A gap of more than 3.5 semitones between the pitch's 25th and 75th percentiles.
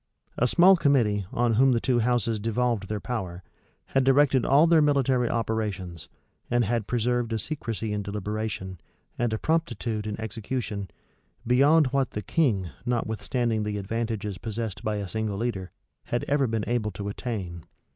No: average, 3.1 semitones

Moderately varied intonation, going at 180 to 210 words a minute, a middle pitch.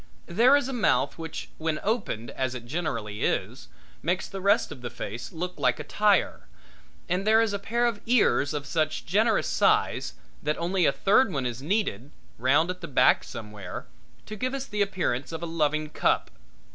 No: wide, 7.0 semitones; average, 190 wpm; medium, 170 Hz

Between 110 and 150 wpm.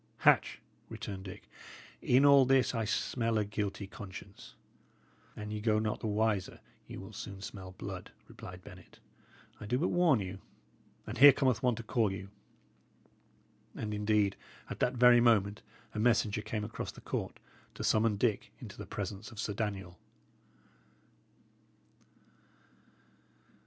Yes: average, 145 wpm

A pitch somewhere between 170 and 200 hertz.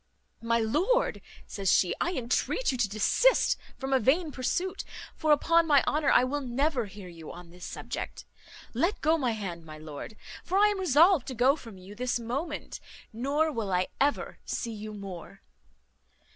No: very high, 255 Hz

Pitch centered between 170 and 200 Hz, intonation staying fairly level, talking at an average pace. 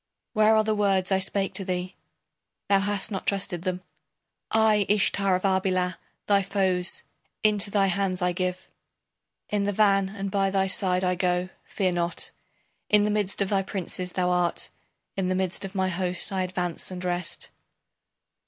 Yes: high, 190 Hz; narrow, 1.6 semitones; average, 170 wpm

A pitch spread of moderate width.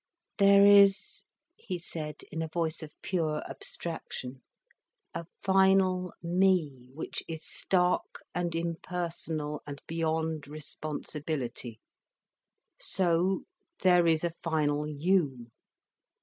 Yes: average, 3.2 semitones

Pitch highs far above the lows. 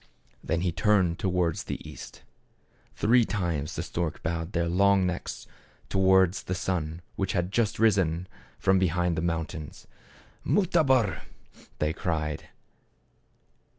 No: average, 2.8 semitones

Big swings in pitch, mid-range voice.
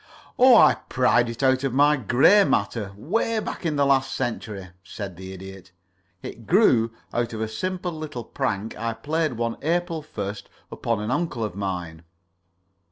No: wide, 6.6 semitones; low, 120 Hz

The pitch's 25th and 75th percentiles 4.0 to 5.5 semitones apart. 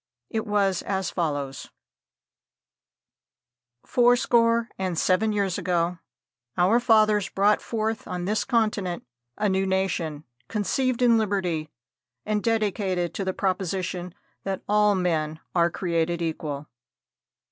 No: average, 3.6 semitones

